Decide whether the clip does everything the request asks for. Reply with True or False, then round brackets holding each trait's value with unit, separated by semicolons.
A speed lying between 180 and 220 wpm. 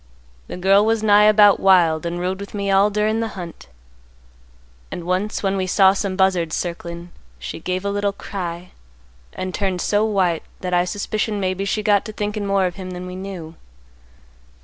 True (185 wpm)